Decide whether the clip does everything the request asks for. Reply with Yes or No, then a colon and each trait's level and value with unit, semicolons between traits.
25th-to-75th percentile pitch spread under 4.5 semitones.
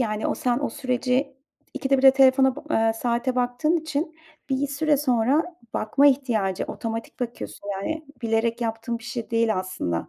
Yes: average, 3.4 semitones